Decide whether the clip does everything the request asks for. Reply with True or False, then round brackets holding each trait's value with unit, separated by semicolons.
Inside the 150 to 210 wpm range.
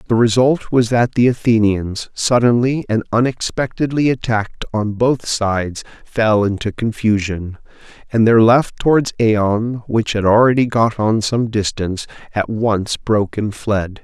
False (140 wpm)